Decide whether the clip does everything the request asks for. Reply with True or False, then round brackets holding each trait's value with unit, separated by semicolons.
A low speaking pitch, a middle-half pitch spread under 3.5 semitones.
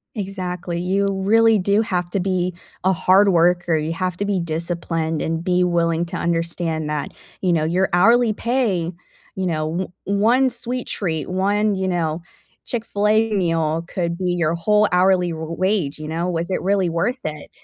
False (180 Hz; 3.1 semitones)